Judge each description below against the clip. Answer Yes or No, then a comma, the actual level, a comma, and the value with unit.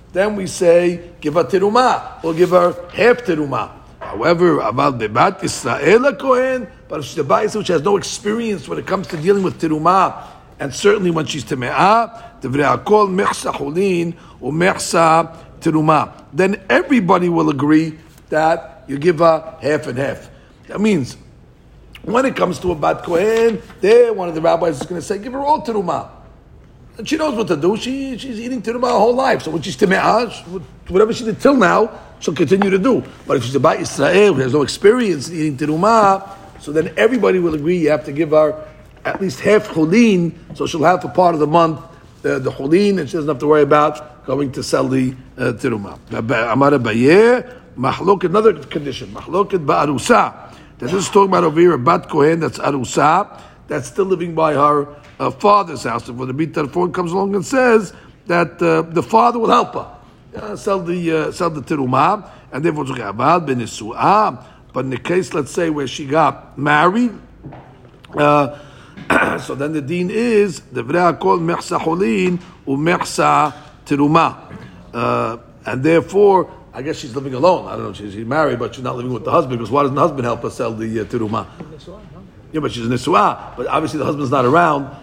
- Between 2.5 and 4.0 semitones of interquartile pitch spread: No, average, 5.1 semitones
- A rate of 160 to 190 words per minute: Yes, average, 185 wpm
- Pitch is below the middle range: No, medium, 165 Hz